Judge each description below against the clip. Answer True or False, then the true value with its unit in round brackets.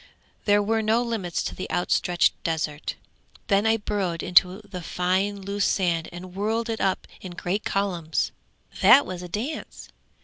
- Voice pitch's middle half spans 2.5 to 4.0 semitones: True (2.9 semitones)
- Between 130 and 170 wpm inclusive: True (160 wpm)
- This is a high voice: True (195 Hz)